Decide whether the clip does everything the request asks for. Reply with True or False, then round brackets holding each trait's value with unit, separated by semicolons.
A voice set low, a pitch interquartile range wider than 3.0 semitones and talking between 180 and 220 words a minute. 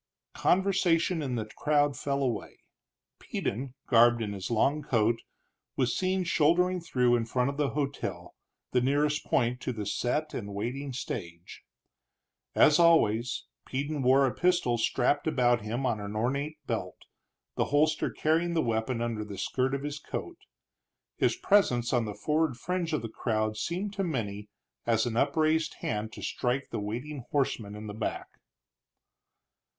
False (130 Hz; 5.0 semitones; 155 wpm)